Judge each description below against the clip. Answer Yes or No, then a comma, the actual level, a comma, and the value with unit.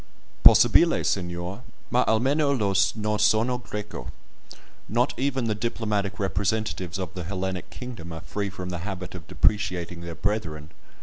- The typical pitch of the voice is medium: No, low, 100 Hz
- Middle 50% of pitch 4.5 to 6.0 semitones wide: No, average, 3.8 semitones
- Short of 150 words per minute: Yes, average, 140 wpm